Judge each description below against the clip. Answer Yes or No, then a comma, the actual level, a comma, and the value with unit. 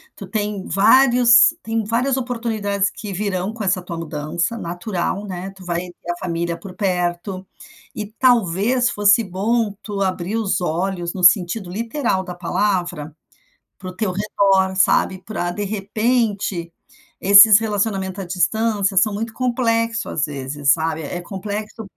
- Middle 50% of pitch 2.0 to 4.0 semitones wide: Yes, average, 3.7 semitones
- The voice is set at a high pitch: Yes, high, 195 Hz